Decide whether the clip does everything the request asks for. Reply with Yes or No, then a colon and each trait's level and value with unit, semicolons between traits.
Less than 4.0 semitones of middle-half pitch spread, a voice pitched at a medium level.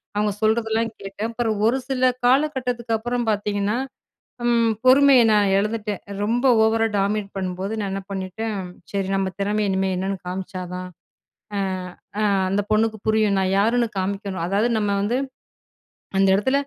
No: average, 2.8 semitones; high, 210 Hz